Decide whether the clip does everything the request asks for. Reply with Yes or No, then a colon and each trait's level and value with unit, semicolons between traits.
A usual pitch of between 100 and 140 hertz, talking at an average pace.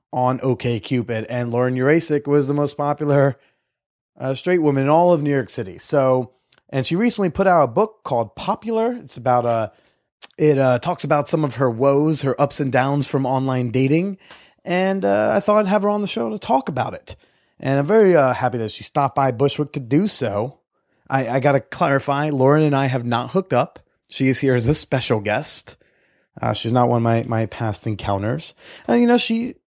No: low, 135 Hz; fast, 210 wpm